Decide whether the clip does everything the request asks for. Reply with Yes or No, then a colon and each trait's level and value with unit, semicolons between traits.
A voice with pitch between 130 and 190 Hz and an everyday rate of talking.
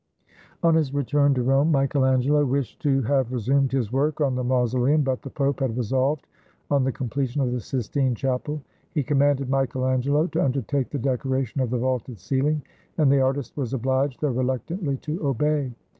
Yes: low, 135 Hz; average, 190 wpm